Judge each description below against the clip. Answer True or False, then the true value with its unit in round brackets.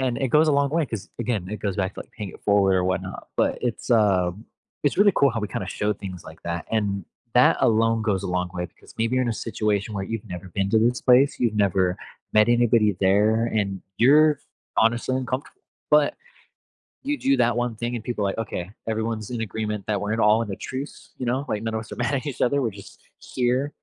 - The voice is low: True (110 Hz)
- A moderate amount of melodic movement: True (3.7 semitones)